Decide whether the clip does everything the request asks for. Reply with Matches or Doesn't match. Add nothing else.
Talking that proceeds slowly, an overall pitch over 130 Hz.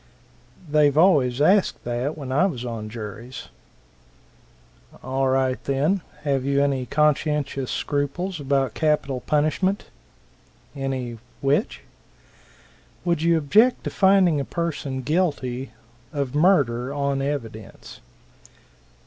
Matches